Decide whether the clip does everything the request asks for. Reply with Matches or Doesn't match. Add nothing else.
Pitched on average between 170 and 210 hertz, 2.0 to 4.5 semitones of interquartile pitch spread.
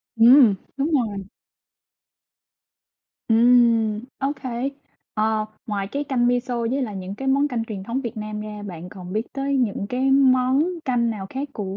Doesn't match